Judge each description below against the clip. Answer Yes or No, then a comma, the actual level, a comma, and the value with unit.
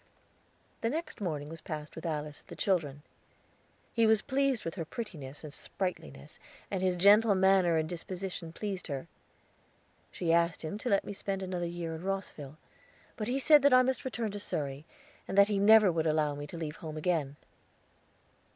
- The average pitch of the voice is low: No, medium, 180 Hz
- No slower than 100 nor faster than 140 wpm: No, average, 185 wpm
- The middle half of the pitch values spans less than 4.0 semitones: No, average, 4.8 semitones